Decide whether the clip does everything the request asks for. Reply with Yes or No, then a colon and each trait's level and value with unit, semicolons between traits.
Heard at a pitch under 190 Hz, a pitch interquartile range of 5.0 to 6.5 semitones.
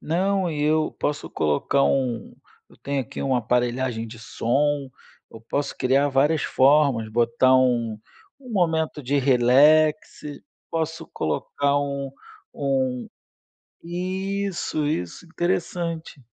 No: medium, 140 Hz; average, 4.3 semitones